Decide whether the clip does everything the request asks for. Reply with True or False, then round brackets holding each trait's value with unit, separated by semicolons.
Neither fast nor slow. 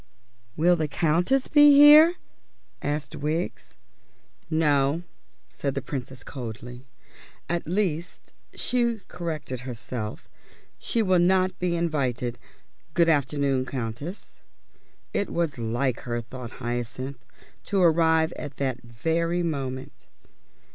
False (105 wpm)